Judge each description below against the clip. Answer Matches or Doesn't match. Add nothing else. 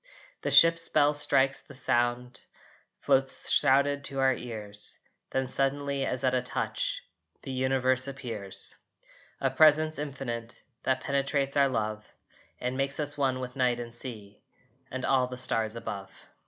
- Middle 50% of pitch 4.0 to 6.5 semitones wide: Doesn't match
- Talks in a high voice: Doesn't match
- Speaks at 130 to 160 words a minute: Matches